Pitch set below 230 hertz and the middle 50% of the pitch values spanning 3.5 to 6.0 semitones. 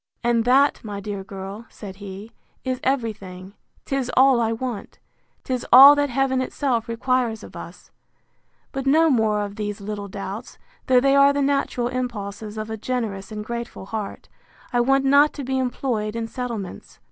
No: high, 235 Hz; average, 3.9 semitones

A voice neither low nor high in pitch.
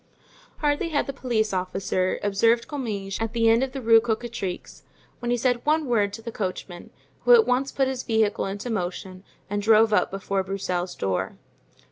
No: high, 225 Hz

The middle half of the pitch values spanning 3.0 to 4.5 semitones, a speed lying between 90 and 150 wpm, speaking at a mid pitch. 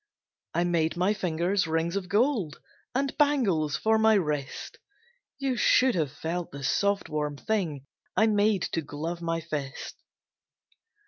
No: wide, 5.4 semitones; average, 140 wpm; medium, 175 Hz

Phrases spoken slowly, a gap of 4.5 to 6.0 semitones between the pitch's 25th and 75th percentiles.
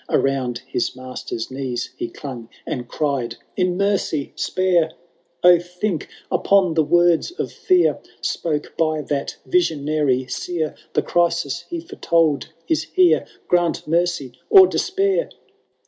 Yes: slow, 130 wpm; average, 5.1 semitones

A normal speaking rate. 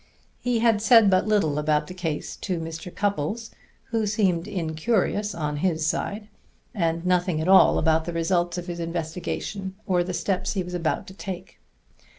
Yes: average, 170 wpm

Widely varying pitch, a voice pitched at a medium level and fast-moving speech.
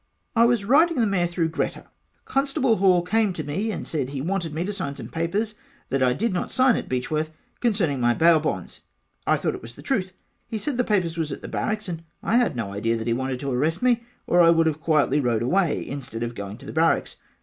Yes: wide, 7.5 semitones; medium, 170 Hz; fast, 240 wpm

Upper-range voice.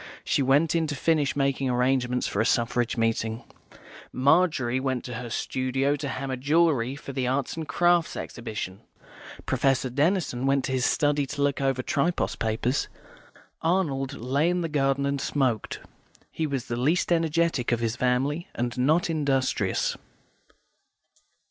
No: low, 135 Hz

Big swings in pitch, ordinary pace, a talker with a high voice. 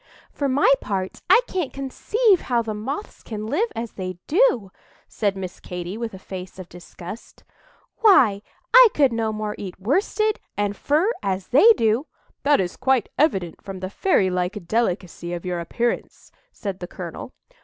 Yes: wide, 7.0 semitones; average, 165 wpm; high, 215 Hz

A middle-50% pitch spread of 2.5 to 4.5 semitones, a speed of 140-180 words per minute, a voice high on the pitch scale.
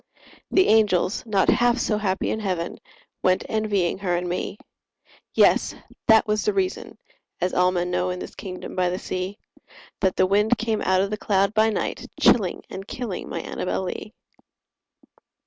Yes: average, 3.0 semitones; average, 165 wpm; high, 195 Hz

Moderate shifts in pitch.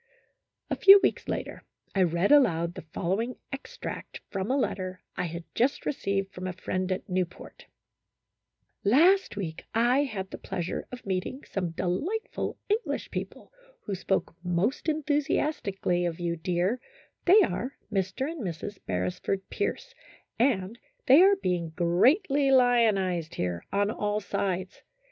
No: wide, 6.8 semitones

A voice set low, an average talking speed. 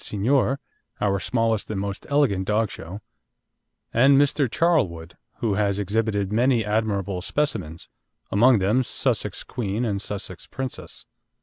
No: low, 105 Hz; slow, 125 wpm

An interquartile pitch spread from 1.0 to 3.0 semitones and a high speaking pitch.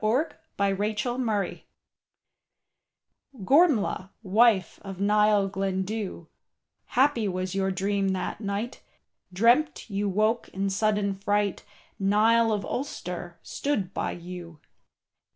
Yes: narrow, 2.6 semitones; high, 205 Hz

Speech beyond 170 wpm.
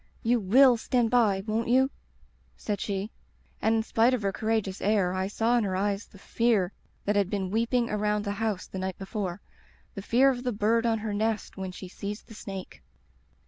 Yes: average, 200 wpm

